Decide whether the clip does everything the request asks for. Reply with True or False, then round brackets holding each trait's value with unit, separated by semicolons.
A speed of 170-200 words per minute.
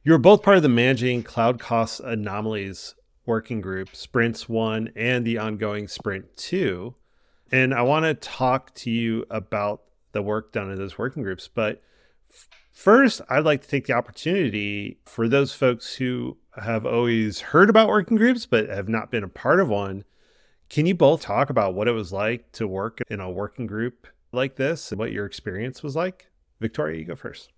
True (190 wpm)